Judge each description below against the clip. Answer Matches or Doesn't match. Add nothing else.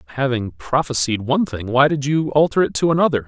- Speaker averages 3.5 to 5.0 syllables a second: Doesn't match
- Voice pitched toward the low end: Matches